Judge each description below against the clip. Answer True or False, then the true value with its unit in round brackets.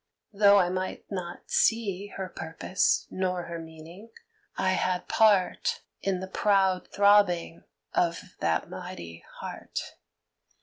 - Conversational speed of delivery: False (120 wpm)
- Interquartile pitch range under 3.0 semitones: True (2.5 semitones)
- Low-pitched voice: False (185 Hz)